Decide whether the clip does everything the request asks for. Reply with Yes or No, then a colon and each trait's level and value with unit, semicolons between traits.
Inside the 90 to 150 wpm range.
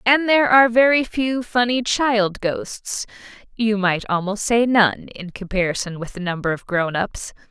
No: average, 160 wpm